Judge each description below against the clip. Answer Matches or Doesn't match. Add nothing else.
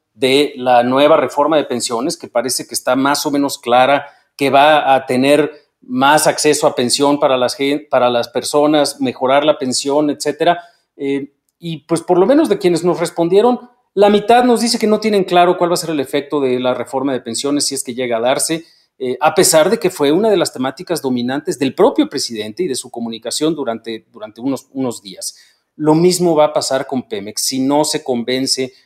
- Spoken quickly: Matches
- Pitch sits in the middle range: Matches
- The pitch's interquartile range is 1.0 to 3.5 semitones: Doesn't match